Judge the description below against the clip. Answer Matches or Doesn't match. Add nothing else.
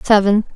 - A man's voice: Doesn't match